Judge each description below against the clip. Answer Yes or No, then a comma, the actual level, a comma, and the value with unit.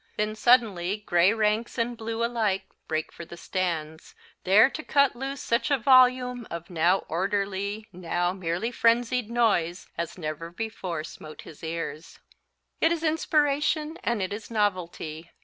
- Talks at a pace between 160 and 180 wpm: No, average, 150 wpm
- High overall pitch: Yes, high, 210 Hz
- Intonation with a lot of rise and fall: Yes, wide, 5.7 semitones